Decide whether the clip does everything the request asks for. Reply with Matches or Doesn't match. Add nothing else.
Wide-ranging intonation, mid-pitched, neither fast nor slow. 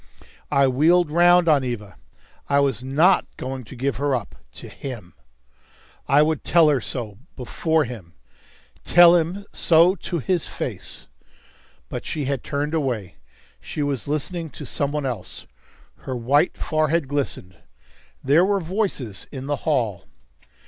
Doesn't match